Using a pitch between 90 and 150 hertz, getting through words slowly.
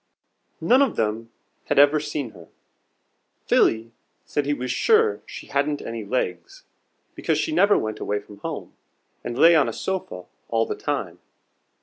No: medium, 140 Hz; average, 155 wpm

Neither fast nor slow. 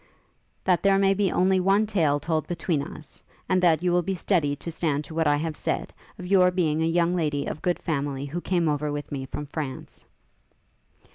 No: fast, 210 wpm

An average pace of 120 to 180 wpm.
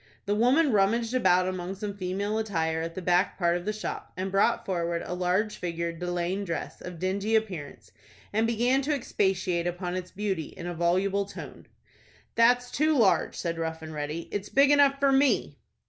No: average, 190 wpm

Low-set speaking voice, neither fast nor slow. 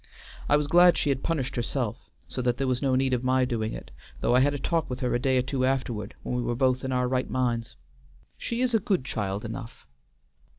No: low, 130 Hz; fast, 245 wpm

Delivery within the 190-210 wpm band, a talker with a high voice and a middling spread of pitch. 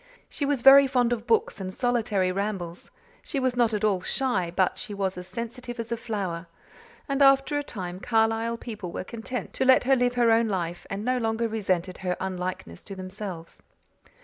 Yes: average, 195 wpm; high, 225 Hz; average, 4.7 semitones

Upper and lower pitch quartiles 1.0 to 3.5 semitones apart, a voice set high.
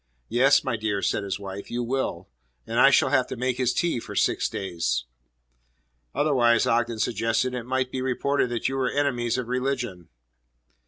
No: average, 2.7 semitones; low, 120 Hz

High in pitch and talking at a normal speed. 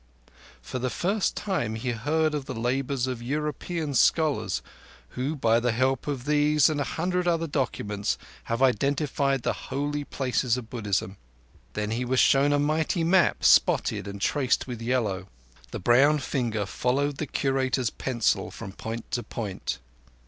No: low, 130 Hz; average, 155 wpm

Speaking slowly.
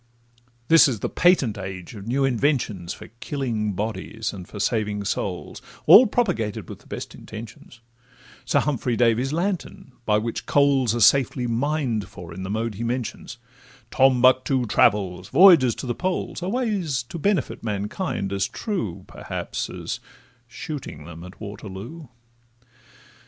No: average, 145 wpm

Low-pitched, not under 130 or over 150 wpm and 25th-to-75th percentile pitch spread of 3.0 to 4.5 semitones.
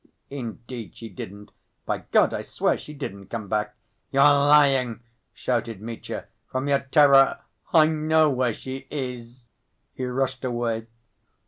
Yes: low, 130 Hz; slow, 135 wpm; average, 3.3 semitones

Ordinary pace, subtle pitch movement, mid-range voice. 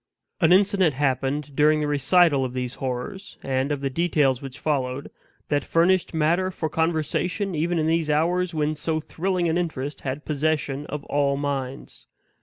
No: average, 165 wpm; average, 3.5 semitones; medium, 150 Hz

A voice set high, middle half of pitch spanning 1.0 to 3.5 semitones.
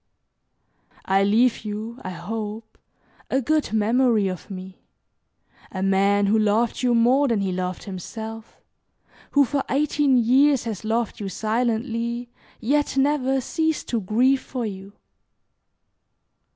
No: high, 225 Hz; average, 4.0 semitones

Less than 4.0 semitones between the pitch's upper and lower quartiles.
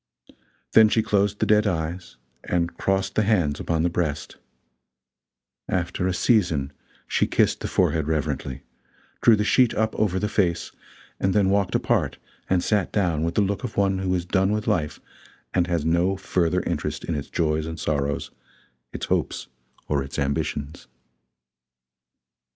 No: average, 4.3 semitones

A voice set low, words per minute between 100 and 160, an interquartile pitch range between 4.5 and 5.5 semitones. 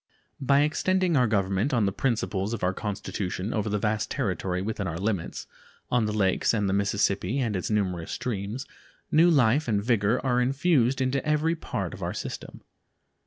No: low, 110 Hz; average, 175 wpm; average, 5.1 semitones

